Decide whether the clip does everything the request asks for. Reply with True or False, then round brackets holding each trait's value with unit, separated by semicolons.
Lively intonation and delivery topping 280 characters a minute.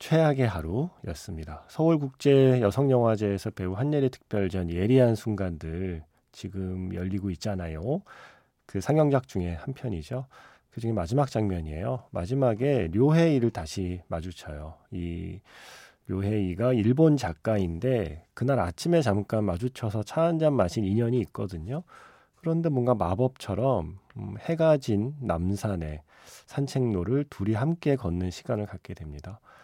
True (6.2 semitones; 295 characters per minute)